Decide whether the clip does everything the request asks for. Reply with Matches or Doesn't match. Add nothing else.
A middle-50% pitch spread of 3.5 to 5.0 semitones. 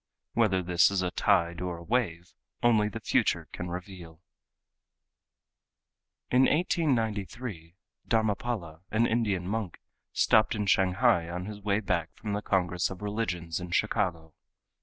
Matches